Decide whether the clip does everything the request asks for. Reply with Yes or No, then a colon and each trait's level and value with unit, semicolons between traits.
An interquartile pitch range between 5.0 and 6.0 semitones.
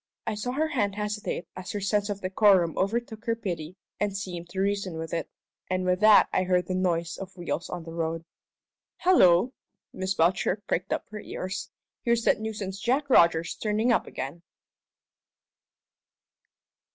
No: average, 3.3 semitones